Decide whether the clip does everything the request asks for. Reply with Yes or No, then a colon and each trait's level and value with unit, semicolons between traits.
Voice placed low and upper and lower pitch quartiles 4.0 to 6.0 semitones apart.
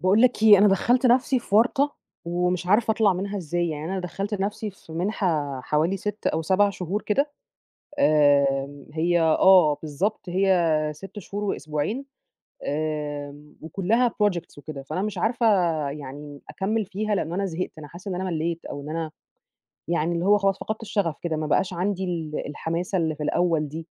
No: medium, 180 Hz; average, 4.8 semitones